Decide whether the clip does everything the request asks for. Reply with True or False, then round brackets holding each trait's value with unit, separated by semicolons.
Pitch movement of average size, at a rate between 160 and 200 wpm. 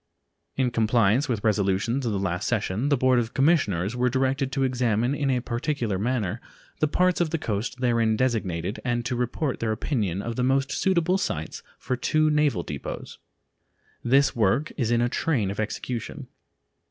True (4.0 semitones; 175 wpm)